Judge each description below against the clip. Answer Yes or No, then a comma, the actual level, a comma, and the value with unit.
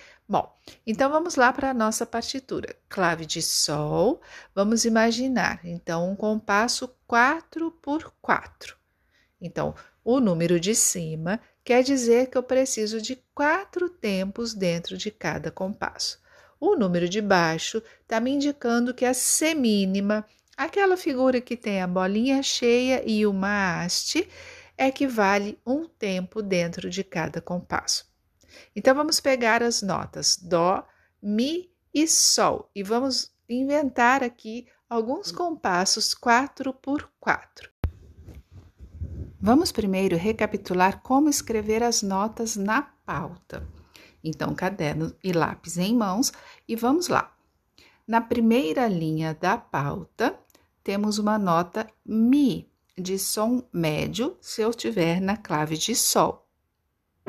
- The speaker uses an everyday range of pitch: No, wide, 5.7 semitones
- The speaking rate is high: Yes, fast, 125 wpm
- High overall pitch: Yes, high, 225 Hz